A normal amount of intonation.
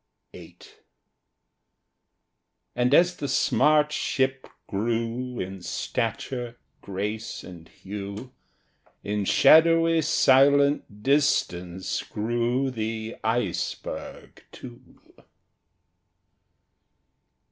Yes: average, 4.9 semitones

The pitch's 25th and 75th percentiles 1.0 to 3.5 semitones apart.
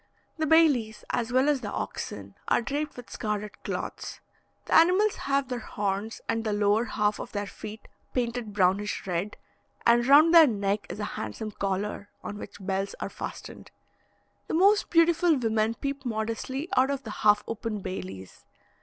No: average, 5.1 semitones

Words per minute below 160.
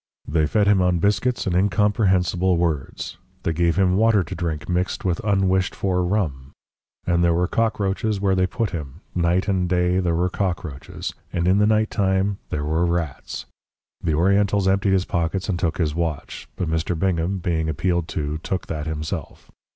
No: average, 180 wpm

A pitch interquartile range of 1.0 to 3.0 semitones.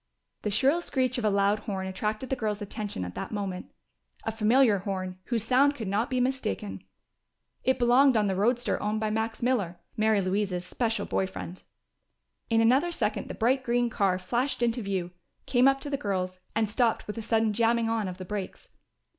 No: average, 3.6 semitones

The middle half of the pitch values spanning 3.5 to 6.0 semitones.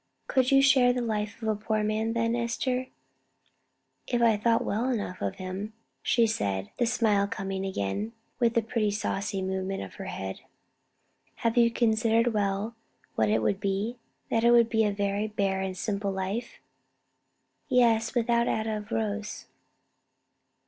No: average, 2.9 semitones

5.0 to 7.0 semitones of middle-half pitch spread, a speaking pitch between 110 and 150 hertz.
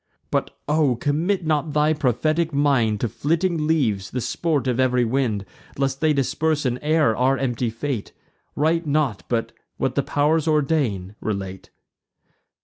No: average, 4.3 semitones; medium, 140 Hz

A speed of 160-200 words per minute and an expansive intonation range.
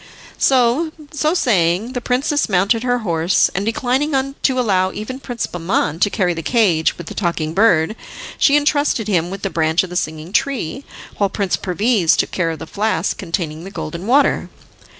Yes: average, 175 wpm; wide, 6.4 semitones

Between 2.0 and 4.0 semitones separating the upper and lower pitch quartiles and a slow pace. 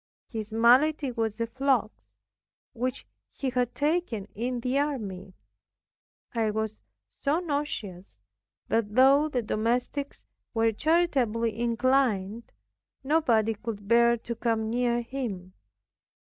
Yes: average, 3.6 semitones; slow, 110 wpm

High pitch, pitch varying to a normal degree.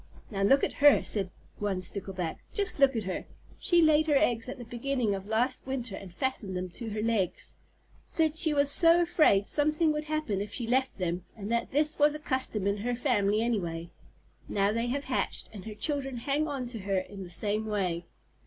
No: high, 230 Hz; wide, 6.1 semitones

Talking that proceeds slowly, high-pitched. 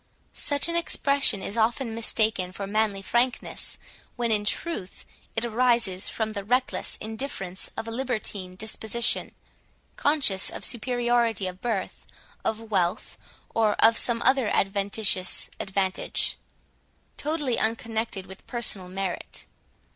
Yes: slow, 120 wpm; high, 220 Hz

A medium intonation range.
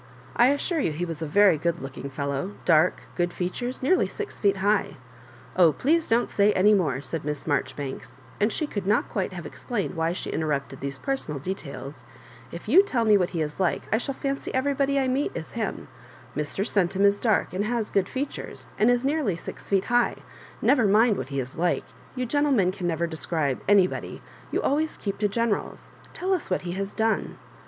No: wide, 6.8 semitones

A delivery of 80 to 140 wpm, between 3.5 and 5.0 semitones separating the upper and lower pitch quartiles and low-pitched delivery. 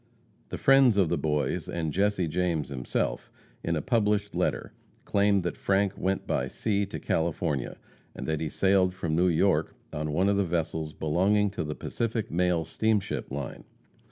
No: average, 170 wpm; average, 4.2 semitones; very low, 90 Hz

